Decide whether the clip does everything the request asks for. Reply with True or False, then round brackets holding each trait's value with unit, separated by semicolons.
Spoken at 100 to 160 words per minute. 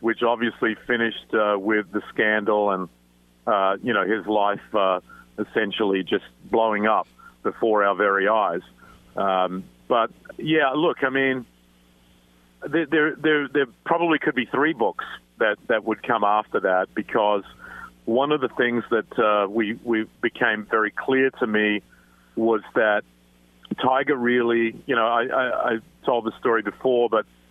True (155 wpm)